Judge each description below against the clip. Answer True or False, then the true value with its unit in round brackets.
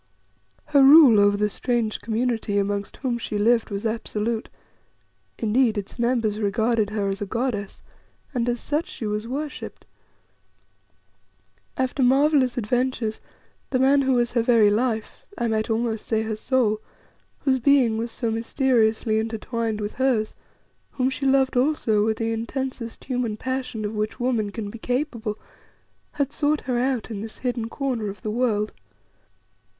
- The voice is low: False (230 Hz)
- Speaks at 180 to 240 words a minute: False (155 wpm)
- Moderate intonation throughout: True (3.0 semitones)